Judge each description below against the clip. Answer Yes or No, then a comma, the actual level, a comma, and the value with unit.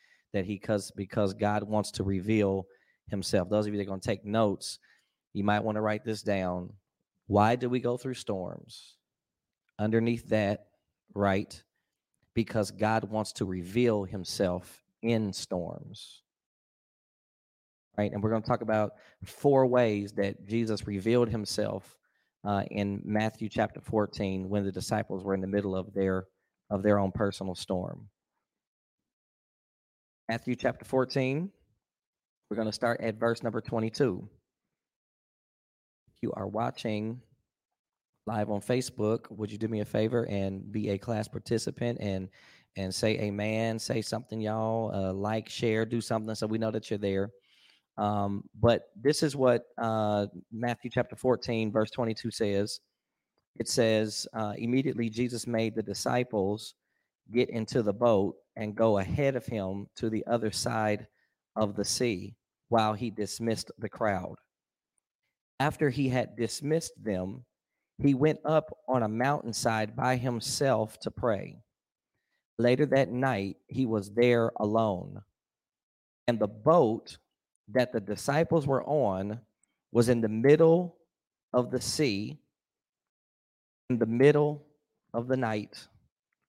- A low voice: Yes, low, 110 Hz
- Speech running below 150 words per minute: Yes, average, 140 wpm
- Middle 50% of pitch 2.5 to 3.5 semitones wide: Yes, average, 2.9 semitones